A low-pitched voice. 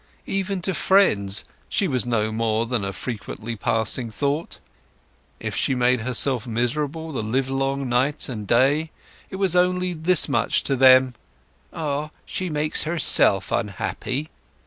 Yes: low, 130 Hz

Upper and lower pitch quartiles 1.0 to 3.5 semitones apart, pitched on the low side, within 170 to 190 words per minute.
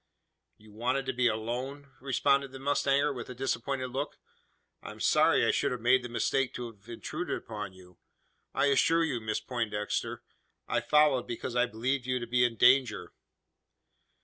Yes: average, 2.8 semitones; low, 125 Hz; average, 175 wpm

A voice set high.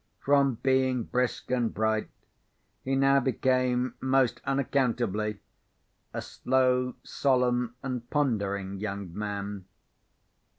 No: low, 125 Hz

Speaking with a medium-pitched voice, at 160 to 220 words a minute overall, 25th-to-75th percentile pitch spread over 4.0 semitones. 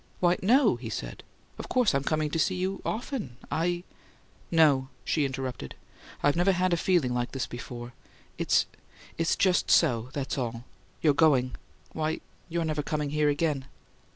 Yes: medium, 150 Hz; average, 165 wpm; average, 5.0 semitones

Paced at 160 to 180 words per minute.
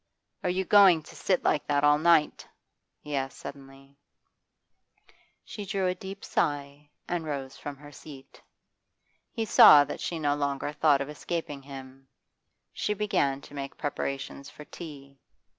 No: average, 150 wpm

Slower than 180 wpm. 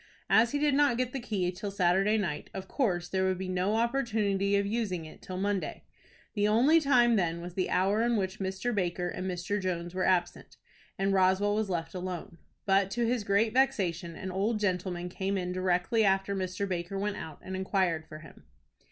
No: average, 200 wpm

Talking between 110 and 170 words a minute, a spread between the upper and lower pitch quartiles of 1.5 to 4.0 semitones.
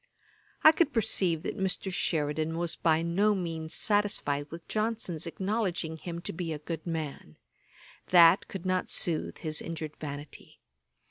Yes: average, 145 wpm; average, 3.2 semitones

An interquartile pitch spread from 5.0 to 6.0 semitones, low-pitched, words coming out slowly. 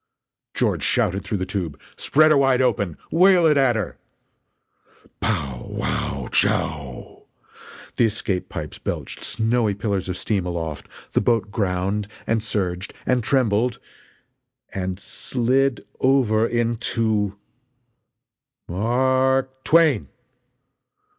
Yes: average, 5.3 semitones; low, 110 Hz; slow, 115 wpm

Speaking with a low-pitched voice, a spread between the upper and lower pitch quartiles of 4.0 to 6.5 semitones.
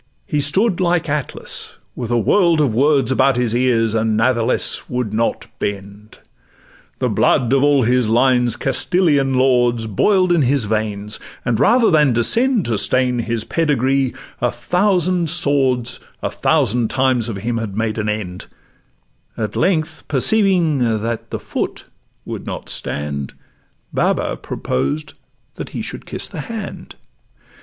Yes: low, 125 Hz; average, 5.1 semitones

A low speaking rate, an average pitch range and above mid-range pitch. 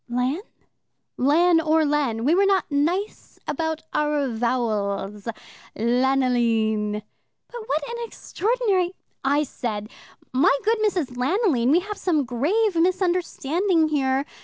No: slow, 120 wpm; wide, 6.6 semitones; very high, 295 Hz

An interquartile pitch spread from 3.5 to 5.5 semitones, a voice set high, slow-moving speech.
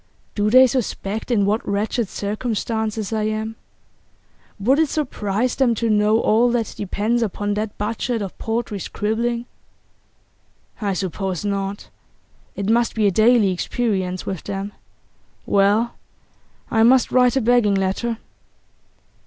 No: average, 2.8 semitones; high, 215 Hz; slow, 130 wpm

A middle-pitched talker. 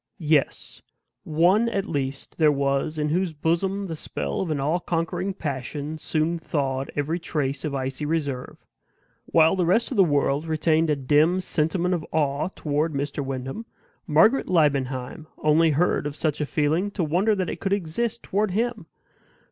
Yes: medium, 155 Hz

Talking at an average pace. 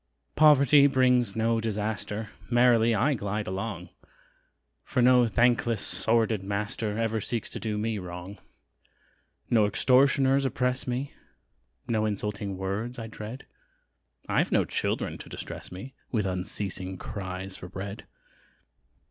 No: slow, 120 wpm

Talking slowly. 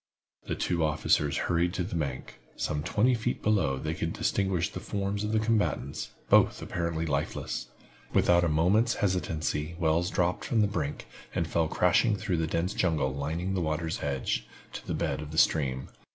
No: average, 180 wpm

